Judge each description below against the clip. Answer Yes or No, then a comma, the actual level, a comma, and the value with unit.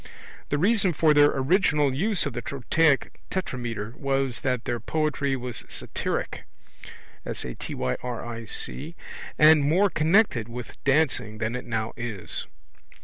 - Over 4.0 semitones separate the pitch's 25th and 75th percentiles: Yes, average, 4.7 semitones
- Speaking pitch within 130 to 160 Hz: Yes, low, 135 Hz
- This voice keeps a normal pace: No, slow, 115 wpm